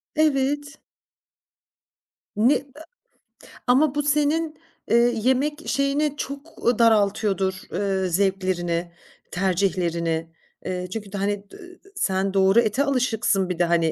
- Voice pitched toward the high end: Yes, high, 205 Hz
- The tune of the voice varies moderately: No, wide, 6.9 semitones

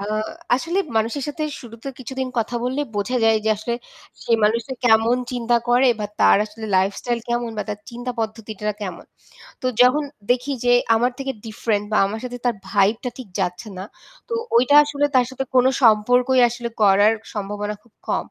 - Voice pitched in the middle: No, high, 235 Hz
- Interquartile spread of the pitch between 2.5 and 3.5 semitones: Yes, average, 2.9 semitones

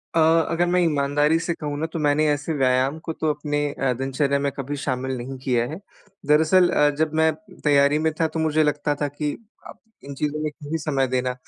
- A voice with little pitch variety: Yes, narrow, 2.3 semitones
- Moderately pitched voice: Yes, medium, 145 Hz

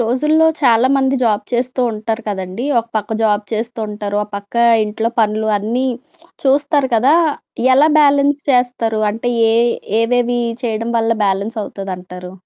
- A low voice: No, high, 230 Hz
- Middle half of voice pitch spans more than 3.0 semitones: Yes, average, 3.4 semitones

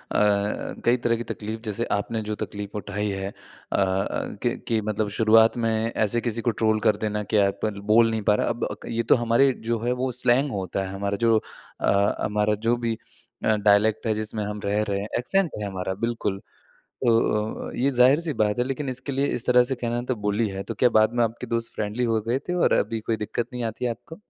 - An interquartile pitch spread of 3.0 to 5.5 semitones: No, narrow, 2.5 semitones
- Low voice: Yes, low, 110 Hz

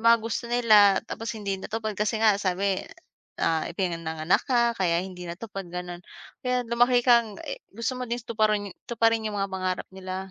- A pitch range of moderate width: Yes, average, 3.8 semitones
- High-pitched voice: Yes, high, 205 Hz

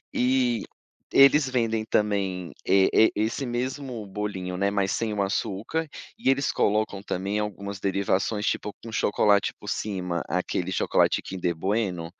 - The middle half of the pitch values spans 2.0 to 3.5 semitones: Yes, average, 3.1 semitones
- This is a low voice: Yes, low, 105 Hz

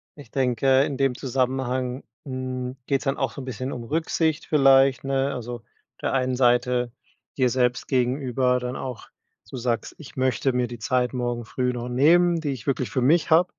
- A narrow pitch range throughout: Yes, narrow, 1.7 semitones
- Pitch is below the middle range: Yes, low, 130 Hz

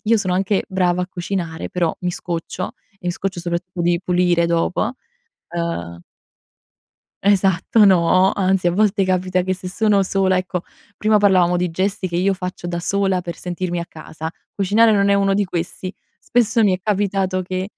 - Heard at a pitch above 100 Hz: Yes, medium, 185 Hz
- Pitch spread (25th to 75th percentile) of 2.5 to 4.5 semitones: No, narrow, 1.9 semitones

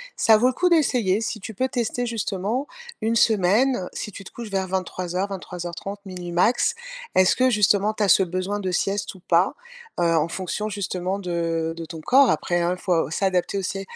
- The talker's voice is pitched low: No, high, 195 Hz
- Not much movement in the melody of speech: No, average, 3.4 semitones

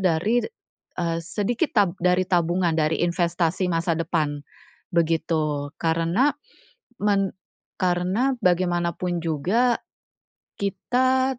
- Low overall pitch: No, medium, 175 Hz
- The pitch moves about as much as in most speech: Yes, average, 3.3 semitones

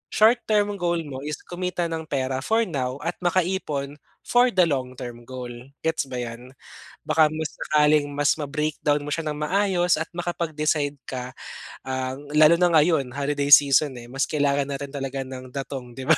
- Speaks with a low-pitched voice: No, medium, 145 Hz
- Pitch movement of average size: Yes, average, 4.0 semitones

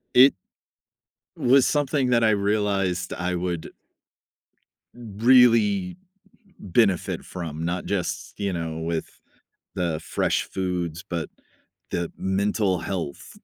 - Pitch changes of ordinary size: Yes, average, 4.8 semitones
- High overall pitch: No, very low, 95 Hz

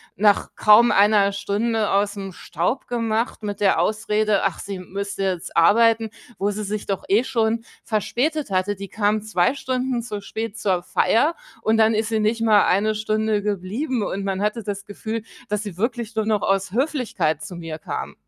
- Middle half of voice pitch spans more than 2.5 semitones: No, narrow, 2.2 semitones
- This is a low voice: No, high, 210 Hz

